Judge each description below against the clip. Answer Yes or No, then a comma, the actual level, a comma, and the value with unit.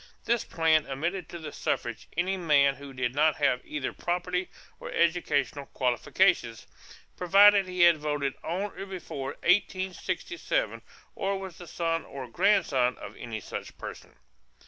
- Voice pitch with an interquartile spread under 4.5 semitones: No, average, 5.0 semitones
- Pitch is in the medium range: Yes, medium, 165 Hz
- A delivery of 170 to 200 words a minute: No, average, 145 wpm